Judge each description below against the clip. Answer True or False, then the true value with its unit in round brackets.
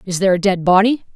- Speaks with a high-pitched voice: True (195 Hz)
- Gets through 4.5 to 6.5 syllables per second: False (7.2 syllables/s)